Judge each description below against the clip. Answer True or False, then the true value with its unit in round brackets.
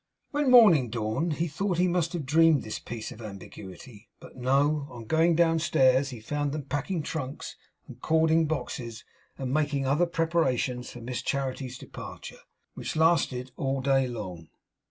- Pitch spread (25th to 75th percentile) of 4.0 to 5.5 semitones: True (4.6 semitones)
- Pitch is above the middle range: False (140 Hz)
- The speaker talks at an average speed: True (155 wpm)